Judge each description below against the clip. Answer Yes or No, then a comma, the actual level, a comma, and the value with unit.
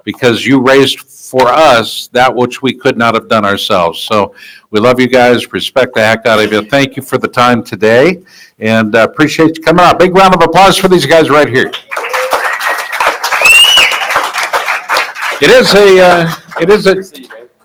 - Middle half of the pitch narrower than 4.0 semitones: No, wide, 5.5 semitones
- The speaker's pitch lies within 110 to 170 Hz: Yes, low, 135 Hz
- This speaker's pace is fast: No, average, 175 wpm